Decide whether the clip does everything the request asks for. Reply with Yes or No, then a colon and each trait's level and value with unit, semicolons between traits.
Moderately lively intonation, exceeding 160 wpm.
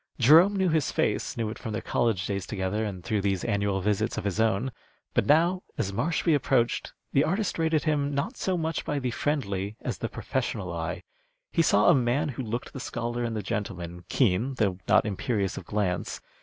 No: wide, 6.3 semitones; average, 200 wpm